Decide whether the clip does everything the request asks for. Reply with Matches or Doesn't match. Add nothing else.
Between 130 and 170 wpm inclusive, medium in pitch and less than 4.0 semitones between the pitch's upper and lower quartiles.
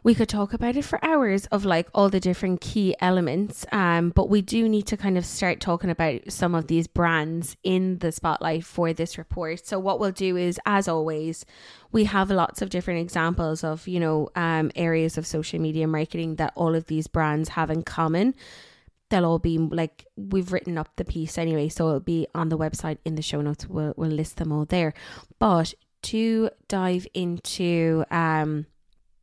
Doesn't match